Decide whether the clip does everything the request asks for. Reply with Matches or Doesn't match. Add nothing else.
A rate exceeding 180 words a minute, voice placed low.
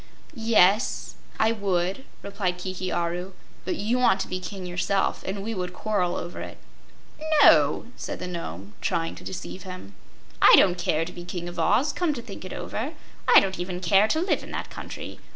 Doesn't match